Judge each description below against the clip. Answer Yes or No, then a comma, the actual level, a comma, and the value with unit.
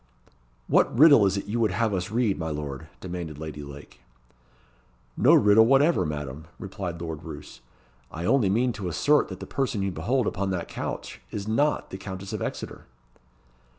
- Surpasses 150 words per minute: Yes, average, 175 wpm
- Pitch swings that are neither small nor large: No, wide, 5.8 semitones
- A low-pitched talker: Yes, very low, 95 Hz